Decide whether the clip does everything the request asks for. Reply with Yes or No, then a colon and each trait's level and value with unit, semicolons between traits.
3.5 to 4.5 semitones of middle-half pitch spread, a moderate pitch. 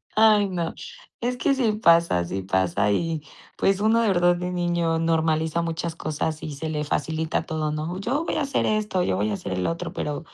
Yes: average, 4.2 semitones; medium, 165 Hz